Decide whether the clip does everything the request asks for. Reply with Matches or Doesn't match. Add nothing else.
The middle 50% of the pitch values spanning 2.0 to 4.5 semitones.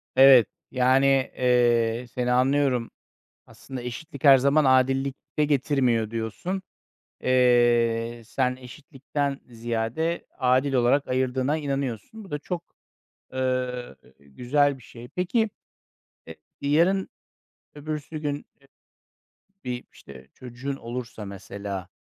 Matches